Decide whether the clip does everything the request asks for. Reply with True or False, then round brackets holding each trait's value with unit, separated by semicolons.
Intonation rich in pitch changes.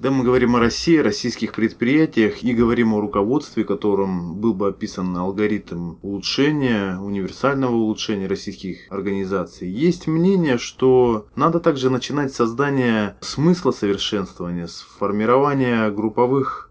False (4.6 semitones)